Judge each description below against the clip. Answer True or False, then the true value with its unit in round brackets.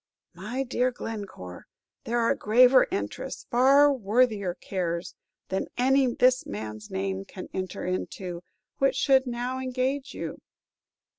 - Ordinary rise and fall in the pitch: False (6.0 semitones)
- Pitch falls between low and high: False (235 Hz)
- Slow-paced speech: True (125 wpm)